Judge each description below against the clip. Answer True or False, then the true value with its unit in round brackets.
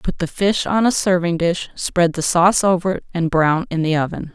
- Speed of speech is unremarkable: False (235 wpm)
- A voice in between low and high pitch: True (175 Hz)